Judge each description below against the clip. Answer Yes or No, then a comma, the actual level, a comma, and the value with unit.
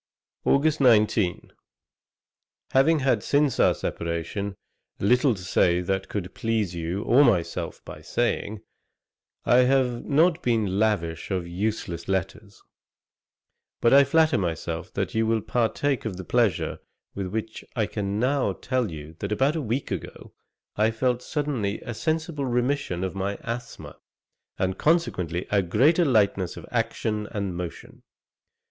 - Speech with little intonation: No, average, 5.3 semitones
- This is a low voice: Yes, low, 110 Hz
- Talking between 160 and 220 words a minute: No, average, 140 wpm